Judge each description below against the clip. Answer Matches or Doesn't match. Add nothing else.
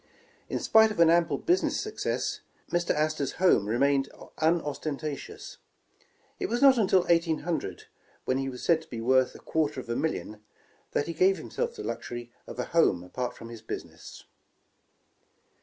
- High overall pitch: Doesn't match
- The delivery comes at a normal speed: Matches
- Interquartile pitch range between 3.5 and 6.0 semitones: Matches